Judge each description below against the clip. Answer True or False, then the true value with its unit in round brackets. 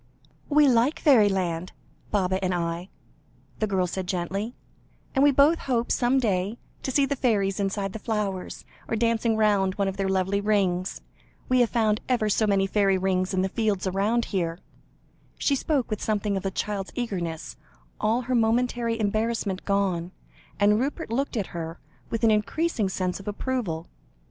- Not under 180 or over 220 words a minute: False (170 wpm)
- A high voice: True (205 Hz)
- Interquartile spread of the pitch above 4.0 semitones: False (3.6 semitones)